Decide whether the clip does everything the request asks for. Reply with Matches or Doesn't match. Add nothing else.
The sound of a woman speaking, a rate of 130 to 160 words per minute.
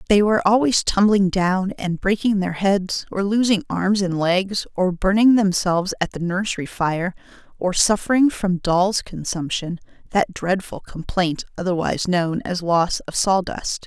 Matches